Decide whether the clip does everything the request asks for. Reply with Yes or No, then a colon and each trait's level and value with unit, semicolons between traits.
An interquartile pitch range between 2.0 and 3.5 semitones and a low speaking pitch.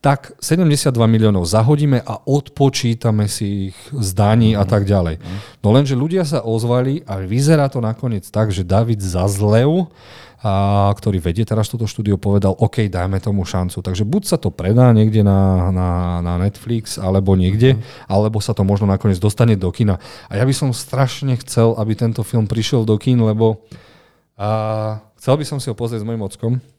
No: average, 4.0 semitones; low, 110 Hz